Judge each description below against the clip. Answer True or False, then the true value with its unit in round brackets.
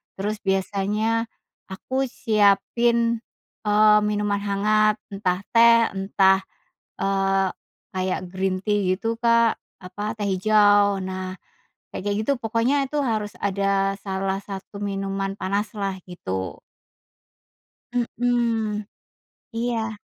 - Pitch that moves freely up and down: False (2.4 semitones)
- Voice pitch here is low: False (205 Hz)